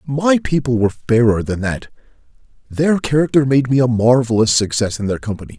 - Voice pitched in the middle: No, low, 125 Hz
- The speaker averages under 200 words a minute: Yes, average, 160 wpm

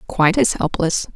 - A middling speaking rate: Yes, average, 155 wpm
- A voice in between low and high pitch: Yes, medium, 180 Hz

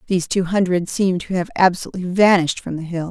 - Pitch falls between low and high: Yes, medium, 180 Hz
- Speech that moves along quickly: Yes, fast, 210 wpm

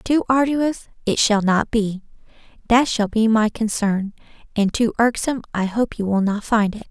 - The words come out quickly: No, average, 175 wpm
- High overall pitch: Yes, high, 220 Hz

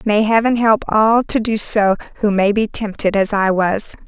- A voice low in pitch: No, high, 210 Hz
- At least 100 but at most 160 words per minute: No, fast, 205 wpm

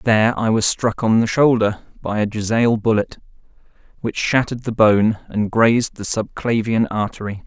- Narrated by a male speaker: Yes, male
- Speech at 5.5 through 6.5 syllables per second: No, 5.0 syllables/s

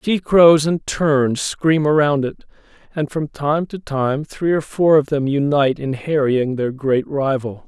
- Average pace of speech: Yes, average, 180 wpm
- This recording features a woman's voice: No, male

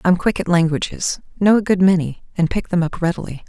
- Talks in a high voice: No, medium, 180 Hz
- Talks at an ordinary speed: No, fast, 225 wpm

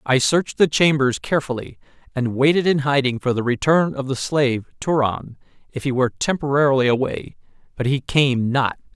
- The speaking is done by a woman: No, male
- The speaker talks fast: No, average, 170 wpm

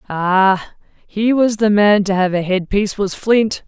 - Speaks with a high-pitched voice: Yes, high, 200 Hz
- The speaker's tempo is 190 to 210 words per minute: No, average, 180 wpm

